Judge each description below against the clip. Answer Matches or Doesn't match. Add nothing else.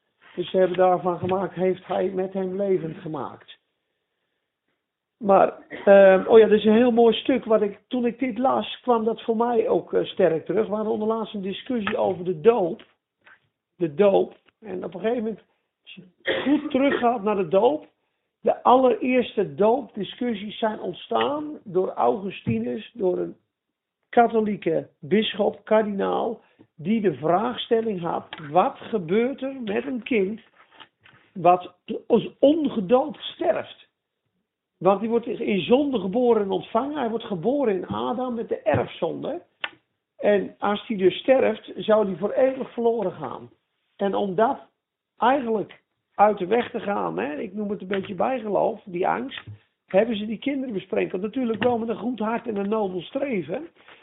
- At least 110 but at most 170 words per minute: Matches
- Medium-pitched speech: Doesn't match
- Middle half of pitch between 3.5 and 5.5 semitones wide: Matches